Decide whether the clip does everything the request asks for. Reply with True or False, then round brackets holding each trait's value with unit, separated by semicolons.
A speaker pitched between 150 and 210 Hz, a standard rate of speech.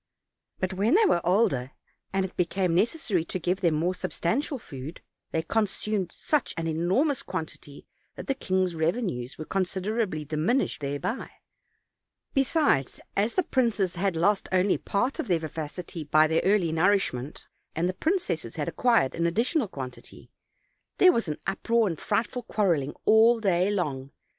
True (185 Hz; 155 wpm)